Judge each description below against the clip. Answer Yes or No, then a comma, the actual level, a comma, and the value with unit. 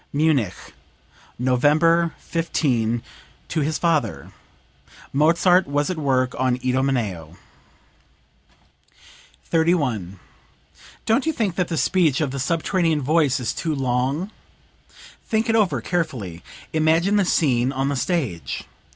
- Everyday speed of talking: No, slow, 115 wpm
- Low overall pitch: No, medium, 150 Hz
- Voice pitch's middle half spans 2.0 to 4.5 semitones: No, average, 4.9 semitones